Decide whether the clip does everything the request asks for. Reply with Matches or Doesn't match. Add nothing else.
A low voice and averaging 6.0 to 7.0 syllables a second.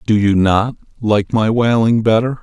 Doesn't match